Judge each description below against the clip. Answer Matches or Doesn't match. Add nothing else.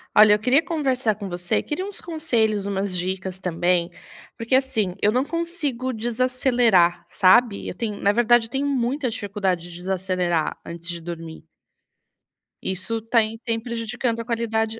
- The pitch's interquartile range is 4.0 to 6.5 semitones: Matches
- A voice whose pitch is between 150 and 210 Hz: Doesn't match